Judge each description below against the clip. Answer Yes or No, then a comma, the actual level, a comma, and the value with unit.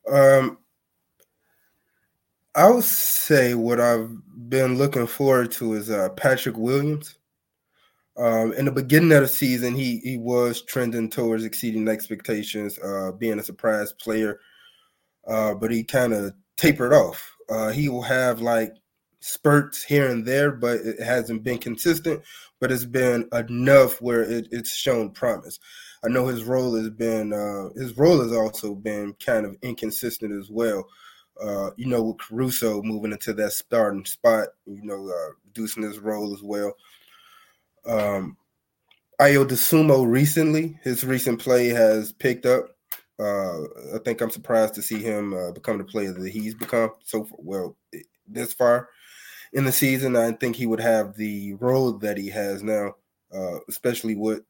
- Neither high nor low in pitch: No, low, 115 Hz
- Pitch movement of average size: Yes, average, 3.0 semitones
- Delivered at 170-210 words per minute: No, average, 160 wpm